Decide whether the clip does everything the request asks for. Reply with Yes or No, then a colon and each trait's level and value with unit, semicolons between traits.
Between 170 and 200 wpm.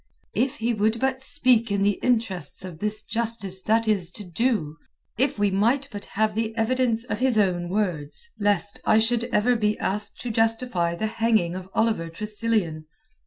Yes: average, 175 wpm